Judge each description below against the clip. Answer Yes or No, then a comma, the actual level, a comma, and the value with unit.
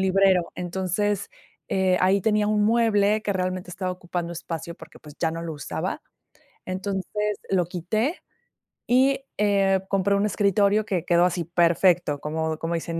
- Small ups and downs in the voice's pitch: No, average, 3.0 semitones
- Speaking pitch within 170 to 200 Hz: Yes, medium, 185 Hz